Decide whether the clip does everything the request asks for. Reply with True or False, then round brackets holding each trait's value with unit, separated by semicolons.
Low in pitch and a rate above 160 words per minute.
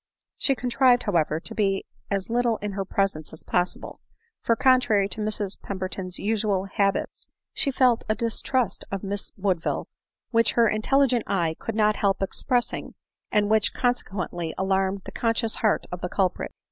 False (205 Hz; 170 wpm)